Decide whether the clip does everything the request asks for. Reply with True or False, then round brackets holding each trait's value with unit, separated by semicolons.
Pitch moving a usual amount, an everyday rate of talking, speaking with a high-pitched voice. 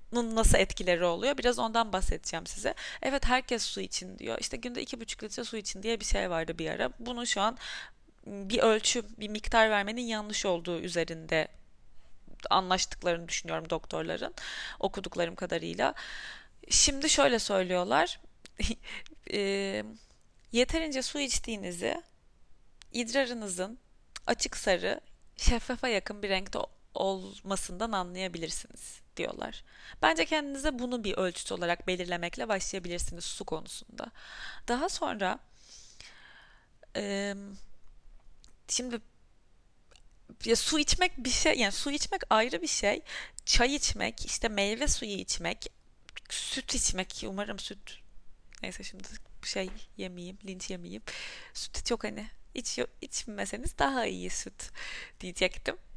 True (4.9 semitones; 115 wpm; 210 Hz)